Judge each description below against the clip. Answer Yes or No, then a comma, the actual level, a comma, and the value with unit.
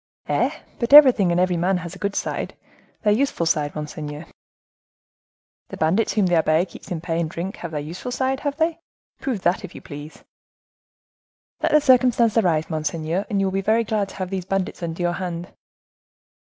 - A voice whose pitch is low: No, medium, 185 Hz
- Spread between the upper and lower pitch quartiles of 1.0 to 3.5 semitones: No, average, 4.9 semitones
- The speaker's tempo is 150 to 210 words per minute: Yes, average, 190 wpm